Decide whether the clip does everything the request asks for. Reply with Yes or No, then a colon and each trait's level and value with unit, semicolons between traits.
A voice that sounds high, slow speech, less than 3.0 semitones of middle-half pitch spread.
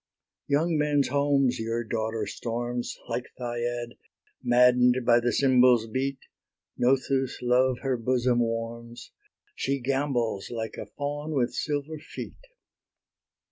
No: low, 125 Hz; slow, 115 wpm; narrow, 2.6 semitones